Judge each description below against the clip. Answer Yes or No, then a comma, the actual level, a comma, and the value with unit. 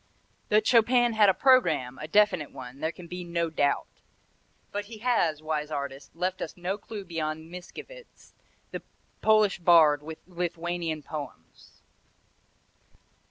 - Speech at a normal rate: No, slow, 130 wpm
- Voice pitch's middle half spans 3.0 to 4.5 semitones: No, average, 5.0 semitones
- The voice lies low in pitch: No, medium, 175 Hz